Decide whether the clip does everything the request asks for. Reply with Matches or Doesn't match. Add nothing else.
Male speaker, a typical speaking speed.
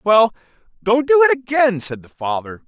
Matches